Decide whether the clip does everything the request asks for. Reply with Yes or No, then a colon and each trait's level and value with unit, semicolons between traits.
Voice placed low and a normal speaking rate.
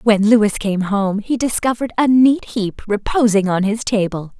No: high, 215 Hz; average, 175 wpm